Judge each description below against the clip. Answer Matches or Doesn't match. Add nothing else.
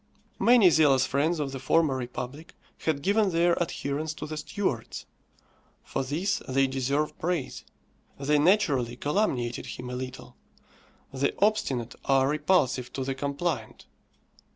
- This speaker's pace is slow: Matches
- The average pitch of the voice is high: Doesn't match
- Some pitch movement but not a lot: Matches